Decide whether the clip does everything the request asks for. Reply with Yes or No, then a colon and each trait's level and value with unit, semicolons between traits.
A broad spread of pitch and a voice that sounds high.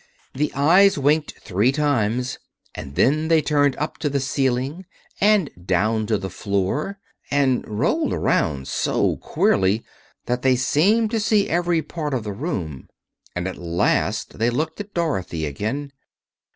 No: wide, 7.1 semitones; low, 135 Hz